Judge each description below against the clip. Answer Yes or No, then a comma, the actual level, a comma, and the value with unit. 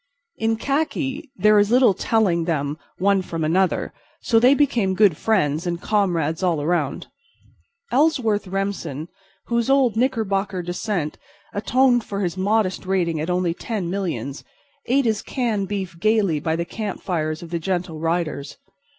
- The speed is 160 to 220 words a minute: No, average, 145 wpm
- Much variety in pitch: No, average, 4.7 semitones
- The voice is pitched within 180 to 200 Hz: Yes, high, 190 Hz